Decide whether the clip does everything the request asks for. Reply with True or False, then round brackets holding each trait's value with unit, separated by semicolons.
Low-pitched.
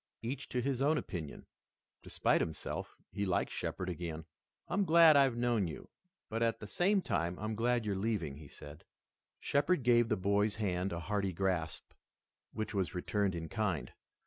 True (105 Hz)